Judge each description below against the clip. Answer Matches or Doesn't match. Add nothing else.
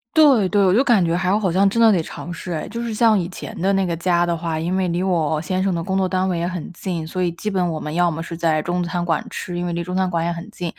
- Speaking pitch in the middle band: Matches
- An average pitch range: Doesn't match